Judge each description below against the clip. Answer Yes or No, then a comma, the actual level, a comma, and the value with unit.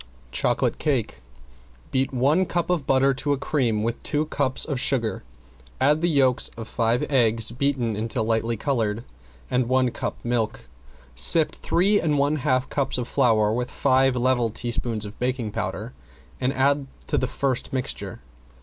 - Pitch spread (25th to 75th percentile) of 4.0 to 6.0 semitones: No, average, 3.2 semitones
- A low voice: Yes, low, 130 Hz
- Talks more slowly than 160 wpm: No, average, 165 wpm